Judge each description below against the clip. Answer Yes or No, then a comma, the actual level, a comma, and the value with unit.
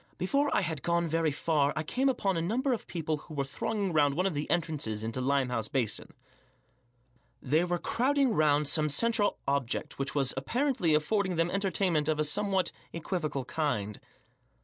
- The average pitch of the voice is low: No, medium, 160 Hz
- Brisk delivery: No, average, 170 wpm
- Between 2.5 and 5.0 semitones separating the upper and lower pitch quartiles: No, wide, 5.4 semitones